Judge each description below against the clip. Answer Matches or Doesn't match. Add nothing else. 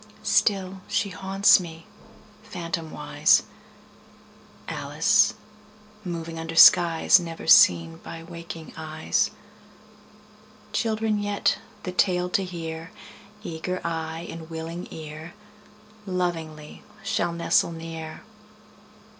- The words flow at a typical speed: Doesn't match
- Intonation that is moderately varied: Doesn't match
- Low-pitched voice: Doesn't match